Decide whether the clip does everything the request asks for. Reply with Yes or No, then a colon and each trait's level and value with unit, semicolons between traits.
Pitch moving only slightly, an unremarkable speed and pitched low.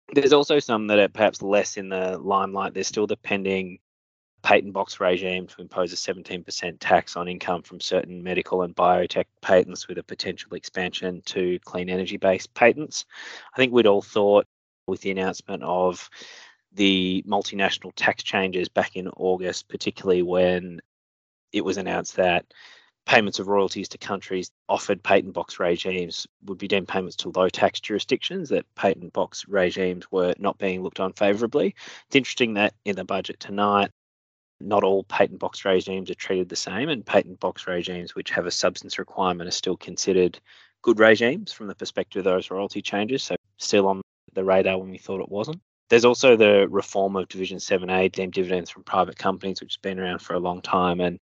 Yes: narrow, 1.8 semitones; average, 185 wpm; very low, 95 Hz